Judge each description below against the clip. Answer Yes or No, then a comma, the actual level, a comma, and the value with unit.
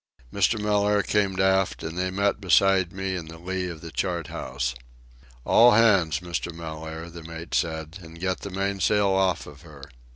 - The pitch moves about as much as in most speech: Yes, average, 3.0 semitones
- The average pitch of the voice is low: Yes, very low, 90 Hz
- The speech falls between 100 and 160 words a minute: No, average, 175 wpm